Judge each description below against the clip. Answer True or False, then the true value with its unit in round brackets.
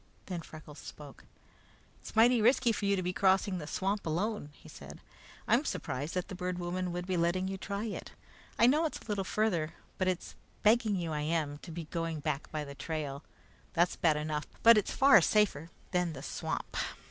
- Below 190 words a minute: False (200 wpm)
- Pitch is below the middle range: False (180 Hz)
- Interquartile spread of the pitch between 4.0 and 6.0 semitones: True (4.4 semitones)